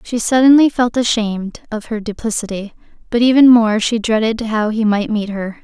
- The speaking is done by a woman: Yes, female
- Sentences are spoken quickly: No, average, 180 wpm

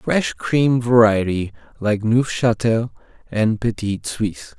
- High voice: No, low, 110 Hz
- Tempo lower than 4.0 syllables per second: Yes, 3.6 syllables/s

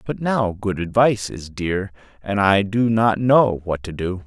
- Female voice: No, male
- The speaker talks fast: No, average, 195 wpm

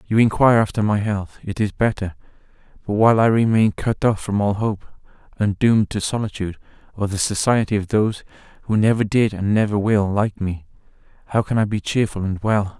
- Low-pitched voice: Yes, low, 105 Hz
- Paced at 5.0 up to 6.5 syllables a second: Yes, 5.6 syllables/s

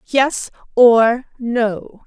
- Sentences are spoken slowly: Yes, slow, 85 wpm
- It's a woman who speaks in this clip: Yes, female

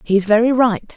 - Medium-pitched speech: No, high, 220 Hz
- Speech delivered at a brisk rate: No, average, 190 wpm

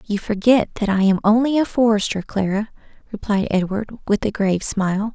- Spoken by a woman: Yes, female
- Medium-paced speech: Yes, average, 175 wpm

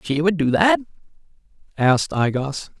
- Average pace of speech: Yes, average, 150 wpm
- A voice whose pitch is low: No, medium, 160 Hz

